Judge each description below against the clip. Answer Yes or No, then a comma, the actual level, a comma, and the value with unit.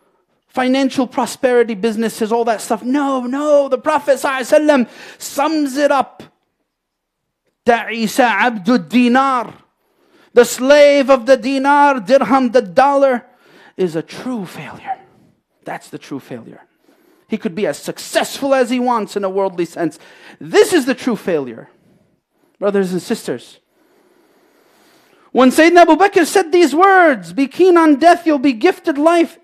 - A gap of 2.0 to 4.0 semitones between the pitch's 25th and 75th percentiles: No, average, 5.3 semitones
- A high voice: Yes, very high, 270 Hz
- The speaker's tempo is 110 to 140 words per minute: Yes, slow, 135 wpm